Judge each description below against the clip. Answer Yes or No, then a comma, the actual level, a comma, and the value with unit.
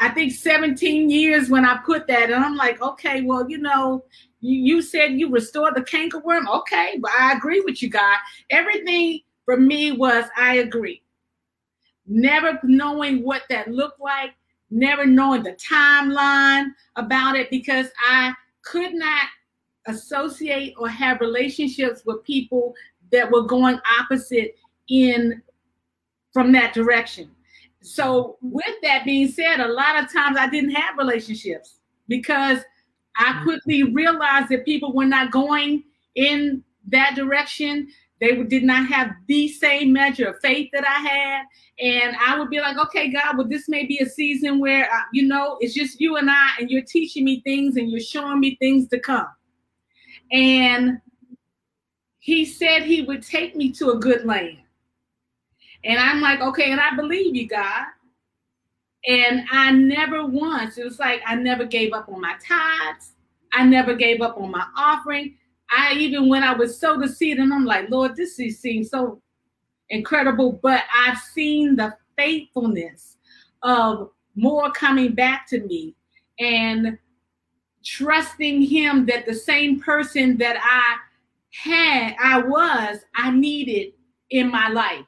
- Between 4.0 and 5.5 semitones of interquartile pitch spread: No, average, 3.0 semitones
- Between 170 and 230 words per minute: No, average, 155 wpm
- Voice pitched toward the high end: Yes, very high, 265 Hz